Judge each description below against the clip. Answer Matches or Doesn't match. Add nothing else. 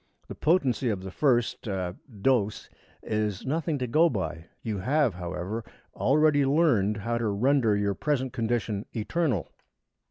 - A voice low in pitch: Matches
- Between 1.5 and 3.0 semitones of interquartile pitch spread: Doesn't match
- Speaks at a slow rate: Doesn't match